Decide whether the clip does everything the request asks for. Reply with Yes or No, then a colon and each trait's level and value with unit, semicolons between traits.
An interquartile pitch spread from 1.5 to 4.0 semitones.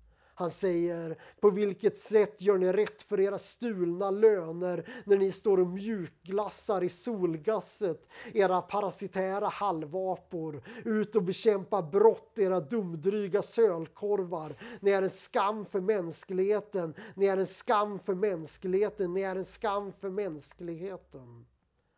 Yes: narrow, 2.4 semitones